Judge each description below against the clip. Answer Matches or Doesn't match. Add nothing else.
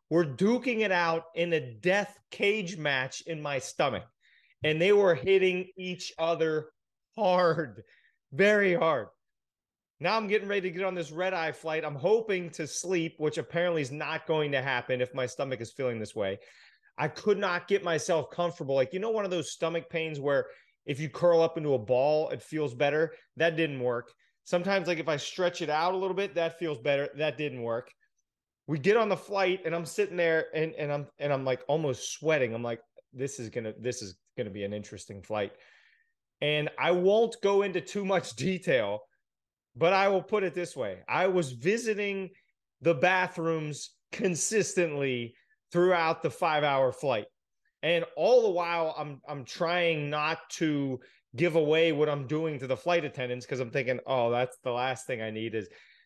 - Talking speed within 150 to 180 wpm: Doesn't match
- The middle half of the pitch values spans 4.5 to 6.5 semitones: Matches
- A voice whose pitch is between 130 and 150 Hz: Doesn't match